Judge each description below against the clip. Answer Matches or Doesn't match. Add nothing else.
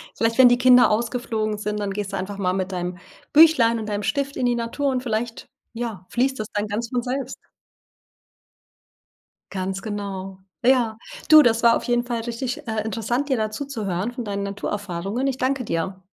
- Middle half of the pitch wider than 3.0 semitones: Matches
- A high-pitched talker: Matches